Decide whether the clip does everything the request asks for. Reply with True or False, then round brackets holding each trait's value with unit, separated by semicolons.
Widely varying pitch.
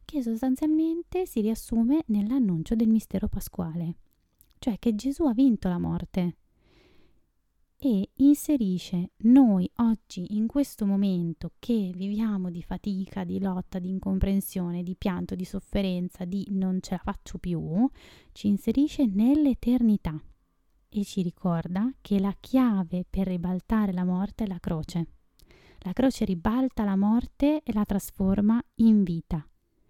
False (4.2 semitones)